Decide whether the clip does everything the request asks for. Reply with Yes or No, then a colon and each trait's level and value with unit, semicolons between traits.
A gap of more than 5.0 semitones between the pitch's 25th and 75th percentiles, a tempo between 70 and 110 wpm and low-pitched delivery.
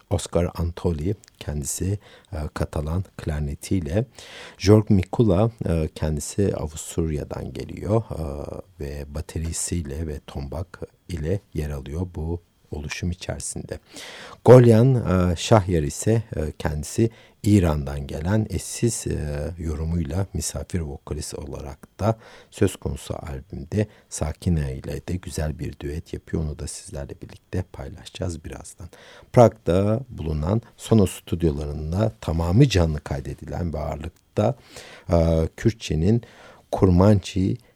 Yes: wide, 5.4 semitones; average, 105 wpm; very low, 85 Hz